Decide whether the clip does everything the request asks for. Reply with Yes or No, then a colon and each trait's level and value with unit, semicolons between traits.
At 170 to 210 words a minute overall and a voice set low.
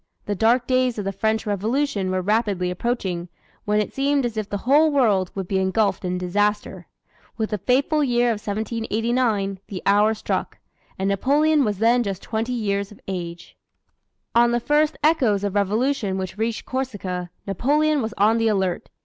No: average, 175 wpm; high, 215 Hz